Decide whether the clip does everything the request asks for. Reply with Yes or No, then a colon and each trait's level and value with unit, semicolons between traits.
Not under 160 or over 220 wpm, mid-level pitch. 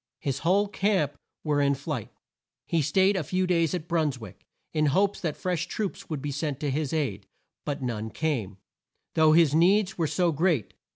Yes: average, 190 wpm; medium, 155 Hz